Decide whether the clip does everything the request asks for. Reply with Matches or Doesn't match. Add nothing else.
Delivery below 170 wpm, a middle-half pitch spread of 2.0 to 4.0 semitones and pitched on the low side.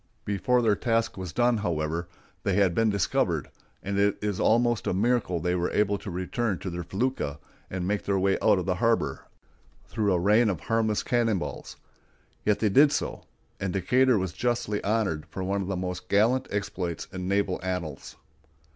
Doesn't match